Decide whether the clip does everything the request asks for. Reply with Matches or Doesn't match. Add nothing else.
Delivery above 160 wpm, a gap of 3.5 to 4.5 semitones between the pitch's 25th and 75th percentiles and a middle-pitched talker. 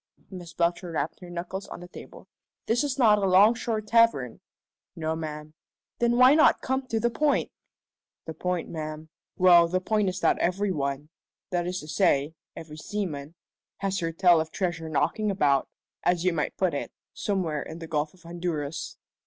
Matches